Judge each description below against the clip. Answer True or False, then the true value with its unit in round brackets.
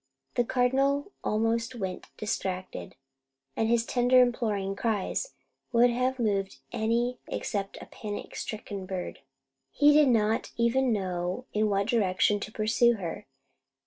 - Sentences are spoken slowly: True (130 wpm)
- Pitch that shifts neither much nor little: True (3.6 semitones)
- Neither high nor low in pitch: False (225 Hz)